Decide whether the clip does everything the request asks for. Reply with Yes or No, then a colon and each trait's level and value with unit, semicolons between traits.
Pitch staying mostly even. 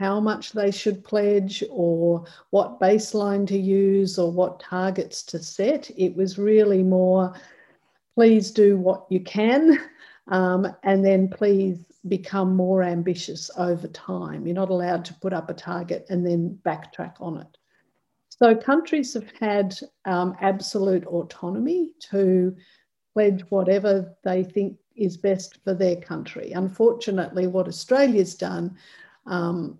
Yes: narrow, 2.1 semitones